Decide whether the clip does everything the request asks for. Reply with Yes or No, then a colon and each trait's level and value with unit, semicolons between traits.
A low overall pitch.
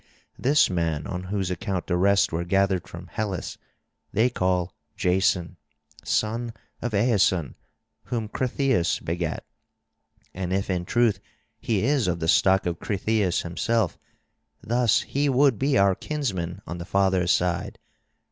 Yes: very low, 95 Hz